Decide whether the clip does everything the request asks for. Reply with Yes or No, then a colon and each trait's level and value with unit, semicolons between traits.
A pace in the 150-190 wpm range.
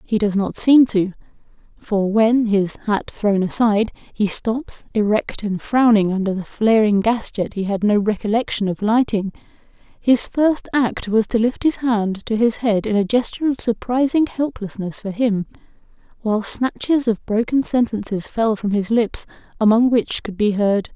Yes: average, 170 wpm